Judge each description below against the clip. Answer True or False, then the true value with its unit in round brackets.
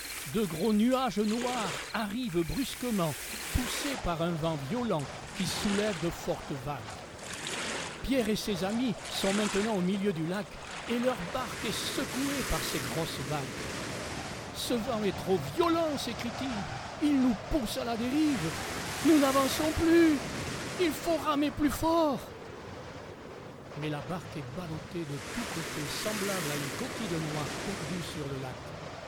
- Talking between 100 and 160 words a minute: True (150 wpm)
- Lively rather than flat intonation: True (6.9 semitones)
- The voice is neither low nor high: False (220 Hz)